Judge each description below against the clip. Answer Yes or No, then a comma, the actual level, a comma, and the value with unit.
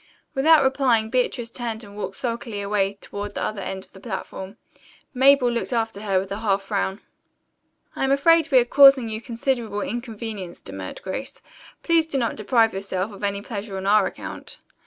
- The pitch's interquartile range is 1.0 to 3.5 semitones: No, average, 4.1 semitones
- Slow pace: No, average, 180 wpm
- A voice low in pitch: No, high, 220 Hz